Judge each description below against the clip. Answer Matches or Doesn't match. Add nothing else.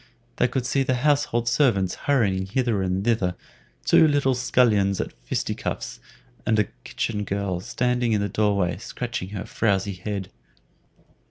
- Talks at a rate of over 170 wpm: Doesn't match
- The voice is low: Matches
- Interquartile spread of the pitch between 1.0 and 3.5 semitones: Doesn't match